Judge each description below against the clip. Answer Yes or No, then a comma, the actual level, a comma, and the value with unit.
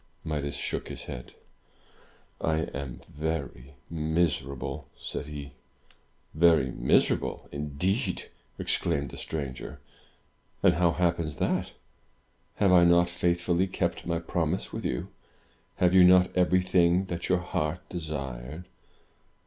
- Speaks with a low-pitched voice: Yes, very low, 85 Hz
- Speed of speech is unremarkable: No, slow, 115 wpm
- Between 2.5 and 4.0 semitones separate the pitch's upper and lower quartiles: Yes, average, 3.5 semitones